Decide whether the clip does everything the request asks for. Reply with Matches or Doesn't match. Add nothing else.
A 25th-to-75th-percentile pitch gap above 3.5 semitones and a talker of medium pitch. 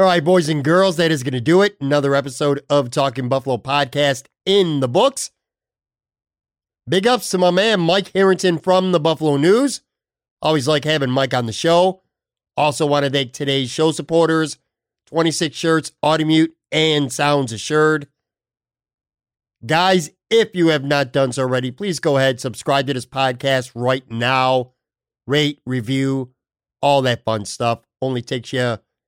Matches